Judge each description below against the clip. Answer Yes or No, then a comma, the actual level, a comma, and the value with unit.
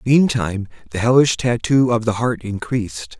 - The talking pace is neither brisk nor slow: Yes, average, 150 wpm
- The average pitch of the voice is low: Yes, low, 115 Hz